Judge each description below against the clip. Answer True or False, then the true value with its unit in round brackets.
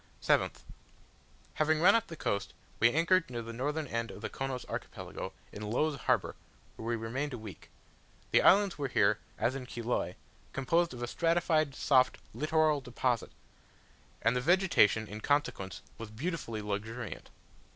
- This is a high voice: False (130 Hz)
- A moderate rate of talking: True (155 wpm)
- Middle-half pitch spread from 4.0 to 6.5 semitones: True (5.6 semitones)